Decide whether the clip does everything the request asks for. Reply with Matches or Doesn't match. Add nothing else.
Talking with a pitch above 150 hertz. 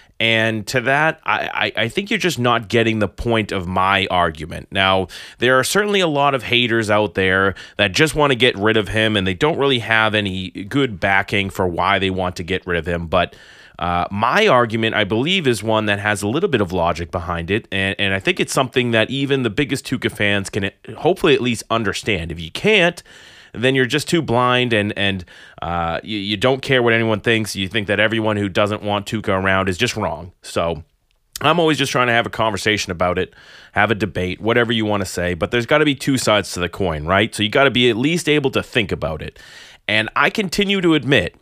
Doesn't match